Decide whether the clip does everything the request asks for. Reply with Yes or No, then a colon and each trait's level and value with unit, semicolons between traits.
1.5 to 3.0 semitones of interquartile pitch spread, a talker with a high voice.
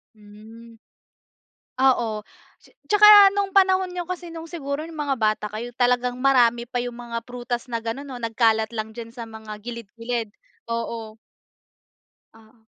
No: average, 3.6 semitones; high, 240 Hz